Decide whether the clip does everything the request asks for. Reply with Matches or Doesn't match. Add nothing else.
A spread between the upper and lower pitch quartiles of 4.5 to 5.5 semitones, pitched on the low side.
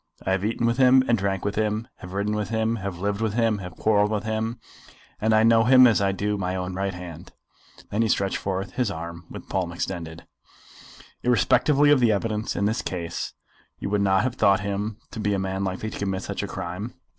Doesn't match